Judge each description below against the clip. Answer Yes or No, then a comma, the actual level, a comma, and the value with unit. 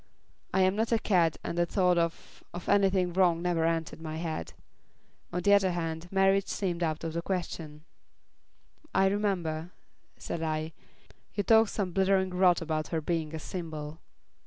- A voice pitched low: No, medium, 175 Hz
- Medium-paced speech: Yes, average, 165 wpm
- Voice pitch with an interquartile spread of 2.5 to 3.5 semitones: Yes, average, 2.9 semitones